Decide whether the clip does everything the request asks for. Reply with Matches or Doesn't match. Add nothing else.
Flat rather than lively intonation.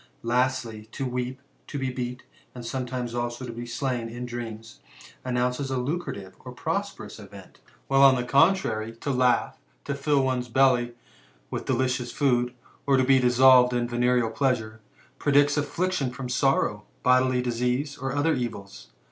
Matches